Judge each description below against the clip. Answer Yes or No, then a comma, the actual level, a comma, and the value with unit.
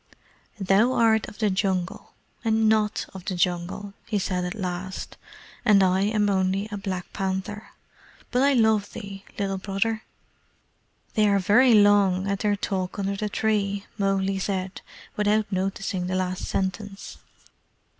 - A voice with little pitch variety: Yes, narrow, 2.0 semitones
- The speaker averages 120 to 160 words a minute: Yes, average, 145 wpm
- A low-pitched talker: No, high, 200 Hz